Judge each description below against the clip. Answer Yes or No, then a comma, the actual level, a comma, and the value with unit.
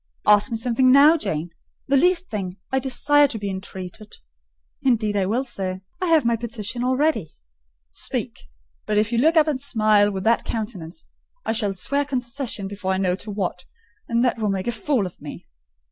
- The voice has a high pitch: Yes, high, 225 Hz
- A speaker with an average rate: Yes, average, 190 wpm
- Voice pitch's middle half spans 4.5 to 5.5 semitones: Yes, average, 5.0 semitones